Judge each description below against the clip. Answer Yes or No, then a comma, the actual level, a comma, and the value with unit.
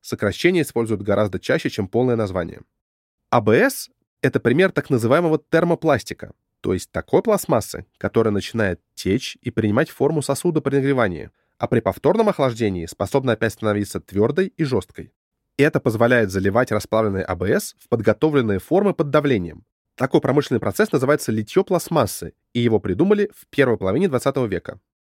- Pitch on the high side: No, low, 120 Hz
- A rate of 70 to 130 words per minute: No, average, 145 wpm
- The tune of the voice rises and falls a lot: Yes, wide, 6.6 semitones